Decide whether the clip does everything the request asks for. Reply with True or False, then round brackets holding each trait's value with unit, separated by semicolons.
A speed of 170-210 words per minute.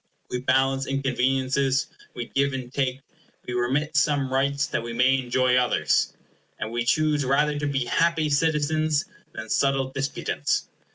False (150 wpm)